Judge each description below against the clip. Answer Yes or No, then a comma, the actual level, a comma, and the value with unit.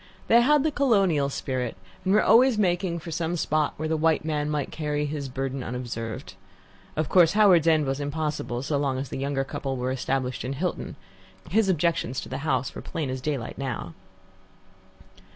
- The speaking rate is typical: Yes, average, 185 wpm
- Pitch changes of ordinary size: Yes, average, 4.2 semitones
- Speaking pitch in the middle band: Yes, medium, 150 Hz